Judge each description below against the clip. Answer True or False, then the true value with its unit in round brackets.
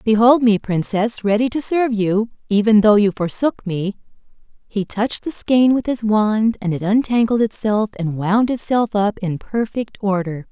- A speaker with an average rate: True (170 wpm)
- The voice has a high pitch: True (215 Hz)